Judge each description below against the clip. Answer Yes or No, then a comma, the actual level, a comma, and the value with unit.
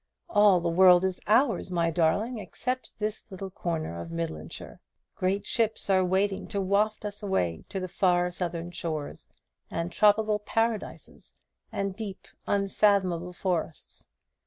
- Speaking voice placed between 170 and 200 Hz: Yes, high, 190 Hz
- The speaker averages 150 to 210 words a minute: No, slow, 135 wpm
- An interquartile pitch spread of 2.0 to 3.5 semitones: Yes, average, 3.2 semitones